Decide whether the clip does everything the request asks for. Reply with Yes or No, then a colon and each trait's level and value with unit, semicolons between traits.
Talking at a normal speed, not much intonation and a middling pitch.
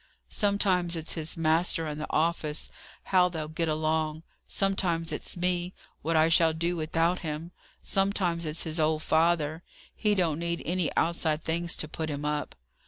Yes: average, 165 wpm; narrow, 1.9 semitones; medium, 165 Hz